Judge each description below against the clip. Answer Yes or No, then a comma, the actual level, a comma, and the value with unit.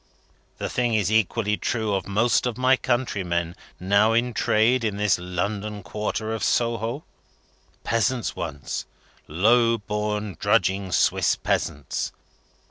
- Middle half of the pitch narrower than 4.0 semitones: Yes, average, 3.0 semitones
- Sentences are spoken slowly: Yes, slow, 125 wpm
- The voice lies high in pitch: No, low, 105 Hz